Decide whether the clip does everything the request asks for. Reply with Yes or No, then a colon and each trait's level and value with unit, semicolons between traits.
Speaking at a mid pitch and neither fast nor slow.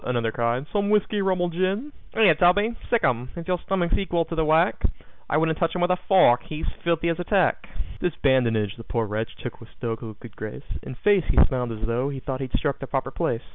No: medium, 155 Hz; fast, 235 wpm